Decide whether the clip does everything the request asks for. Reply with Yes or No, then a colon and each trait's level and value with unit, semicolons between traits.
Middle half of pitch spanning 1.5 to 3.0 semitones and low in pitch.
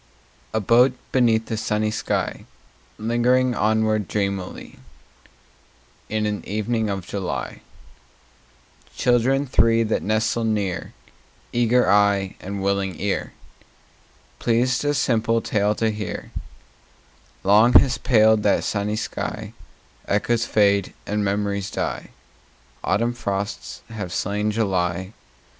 Yes: narrow, 2.4 semitones; low, 110 Hz